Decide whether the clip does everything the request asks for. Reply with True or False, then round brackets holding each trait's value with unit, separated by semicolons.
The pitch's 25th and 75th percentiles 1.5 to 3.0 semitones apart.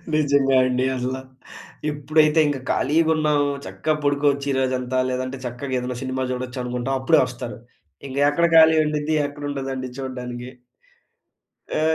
True (2.4 semitones)